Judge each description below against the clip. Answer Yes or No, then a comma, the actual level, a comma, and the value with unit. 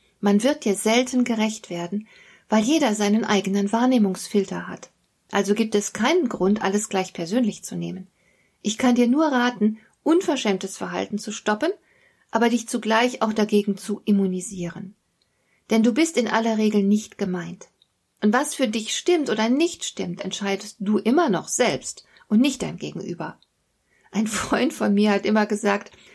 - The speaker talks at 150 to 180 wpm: Yes, average, 160 wpm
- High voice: Yes, high, 215 Hz